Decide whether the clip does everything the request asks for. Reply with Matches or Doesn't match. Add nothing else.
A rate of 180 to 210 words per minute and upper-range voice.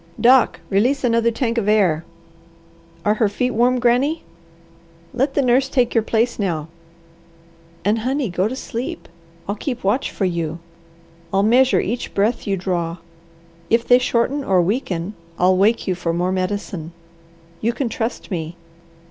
Doesn't match